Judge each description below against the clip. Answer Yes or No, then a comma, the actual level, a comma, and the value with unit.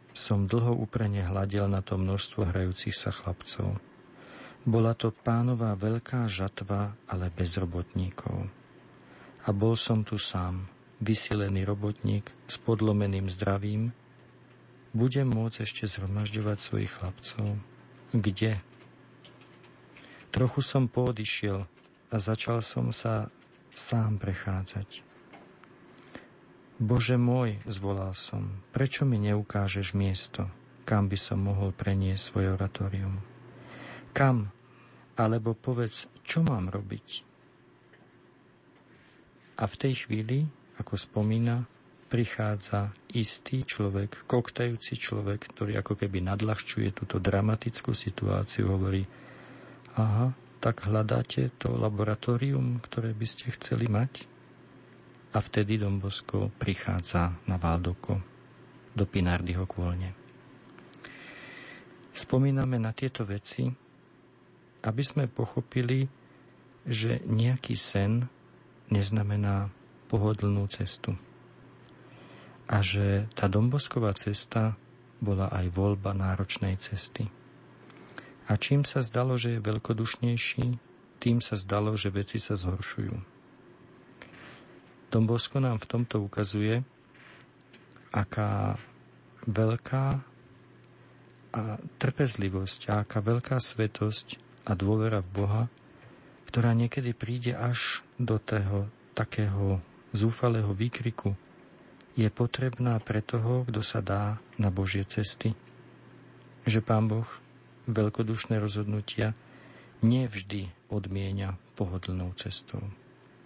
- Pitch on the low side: Yes, low, 110 Hz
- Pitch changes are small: No, average, 3.4 semitones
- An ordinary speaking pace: No, slow, 95 wpm